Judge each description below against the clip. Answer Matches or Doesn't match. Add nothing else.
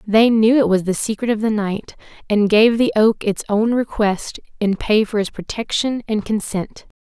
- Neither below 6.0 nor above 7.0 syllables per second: Doesn't match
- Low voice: Doesn't match